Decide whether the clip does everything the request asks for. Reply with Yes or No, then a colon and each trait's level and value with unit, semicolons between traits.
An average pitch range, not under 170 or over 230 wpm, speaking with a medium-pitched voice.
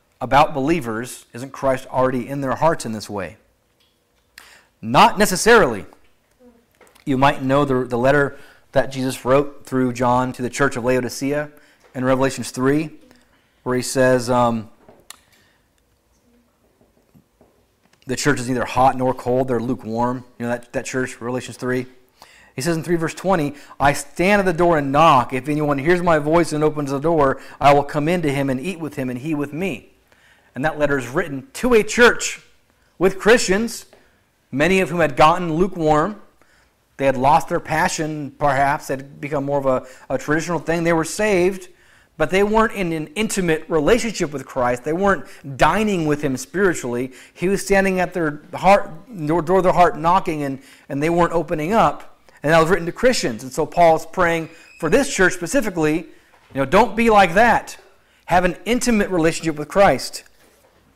Yes: average, 5.0 semitones; average, 175 wpm; medium, 150 Hz